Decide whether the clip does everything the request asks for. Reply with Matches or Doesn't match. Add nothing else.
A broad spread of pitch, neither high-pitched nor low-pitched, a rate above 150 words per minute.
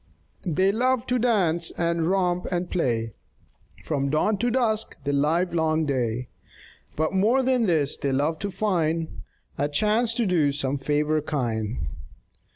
Doesn't match